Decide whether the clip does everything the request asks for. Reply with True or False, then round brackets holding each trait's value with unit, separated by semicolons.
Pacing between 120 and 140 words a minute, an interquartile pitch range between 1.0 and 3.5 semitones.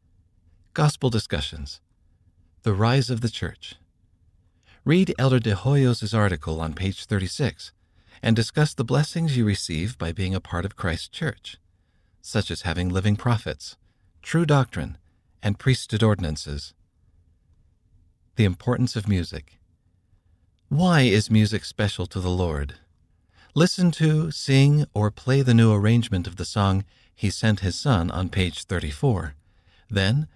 False (135 wpm; 5.1 semitones)